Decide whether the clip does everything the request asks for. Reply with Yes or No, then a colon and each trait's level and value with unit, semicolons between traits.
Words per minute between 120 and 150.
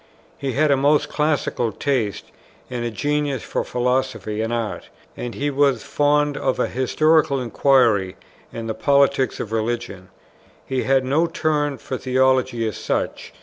Yes: average, 145 wpm